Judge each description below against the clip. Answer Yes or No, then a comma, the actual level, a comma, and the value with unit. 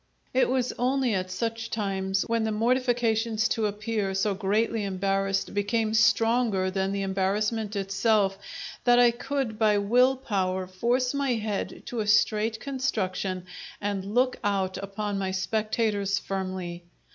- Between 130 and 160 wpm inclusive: Yes, average, 140 wpm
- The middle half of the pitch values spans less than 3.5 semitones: Yes, average, 3.1 semitones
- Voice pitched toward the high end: Yes, high, 210 Hz